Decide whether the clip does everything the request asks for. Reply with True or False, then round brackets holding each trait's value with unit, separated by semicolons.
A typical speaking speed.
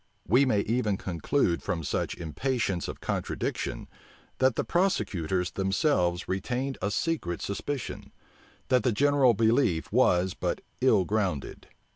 False (125 wpm)